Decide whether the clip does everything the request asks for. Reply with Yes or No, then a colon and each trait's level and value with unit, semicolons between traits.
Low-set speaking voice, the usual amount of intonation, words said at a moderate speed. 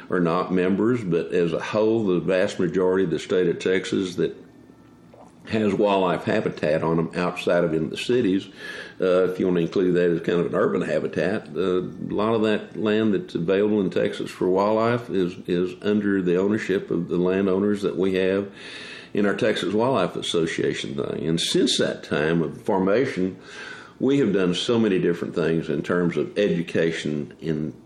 Yes: very low, 90 Hz; average, 3.0 semitones; average, 185 wpm